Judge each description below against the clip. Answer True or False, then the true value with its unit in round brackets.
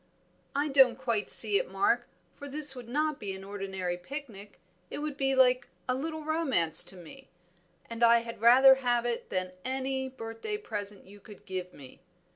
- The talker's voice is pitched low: False (245 Hz)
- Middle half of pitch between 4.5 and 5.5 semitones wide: True (5.1 semitones)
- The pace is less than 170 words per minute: False (180 wpm)